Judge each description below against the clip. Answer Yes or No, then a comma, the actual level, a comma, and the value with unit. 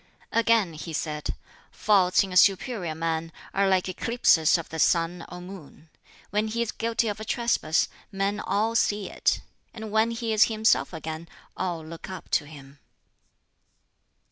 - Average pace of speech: Yes, average, 160 wpm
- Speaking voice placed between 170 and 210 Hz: Yes, high, 190 Hz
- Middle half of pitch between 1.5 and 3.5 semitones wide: No, average, 5.0 semitones